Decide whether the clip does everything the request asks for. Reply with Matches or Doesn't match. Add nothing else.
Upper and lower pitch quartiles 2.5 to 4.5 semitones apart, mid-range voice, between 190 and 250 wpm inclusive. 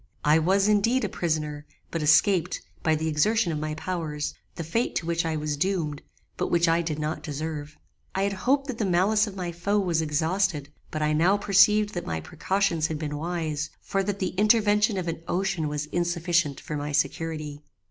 Matches